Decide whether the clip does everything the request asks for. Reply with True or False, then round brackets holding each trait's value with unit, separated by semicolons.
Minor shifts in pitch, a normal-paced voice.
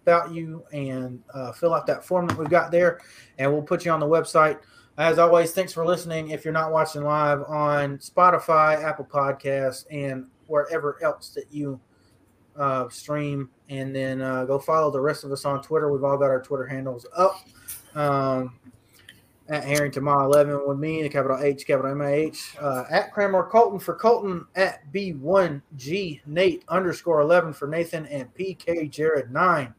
False (3.4 semitones; 175 wpm)